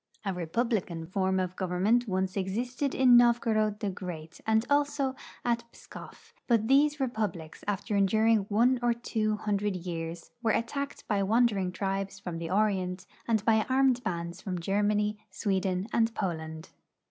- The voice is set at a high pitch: Yes, high, 210 Hz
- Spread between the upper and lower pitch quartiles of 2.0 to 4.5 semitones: Yes, average, 4.1 semitones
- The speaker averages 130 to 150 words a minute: Yes, average, 145 wpm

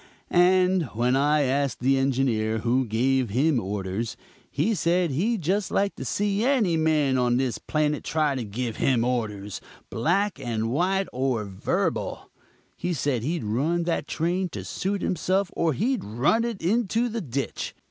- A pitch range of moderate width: No, wide, 7.0 semitones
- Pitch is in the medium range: Yes, medium, 145 Hz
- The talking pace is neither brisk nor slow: Yes, average, 160 wpm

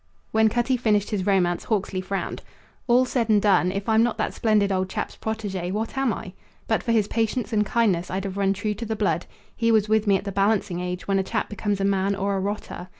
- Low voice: No, high, 205 Hz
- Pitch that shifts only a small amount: Yes, narrow, 2.3 semitones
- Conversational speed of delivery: No, fast, 240 wpm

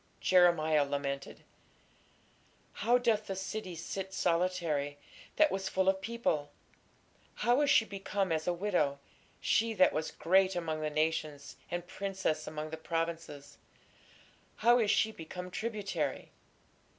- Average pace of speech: No, slow, 130 wpm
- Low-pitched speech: No, medium, 180 Hz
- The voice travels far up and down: No, average, 4.1 semitones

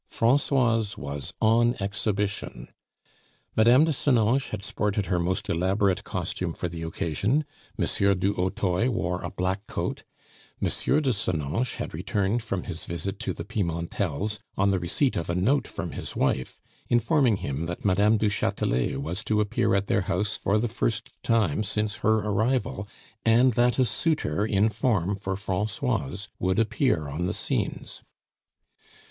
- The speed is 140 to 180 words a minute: Yes, average, 155 wpm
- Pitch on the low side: Yes, low, 100 Hz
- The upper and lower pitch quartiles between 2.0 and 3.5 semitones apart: No, average, 3.9 semitones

